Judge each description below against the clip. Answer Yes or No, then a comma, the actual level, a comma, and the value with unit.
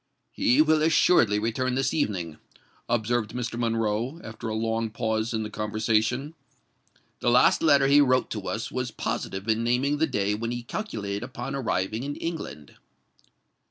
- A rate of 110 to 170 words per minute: Yes, average, 160 wpm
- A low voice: Yes, low, 115 Hz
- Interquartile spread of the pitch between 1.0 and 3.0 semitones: No, average, 3.5 semitones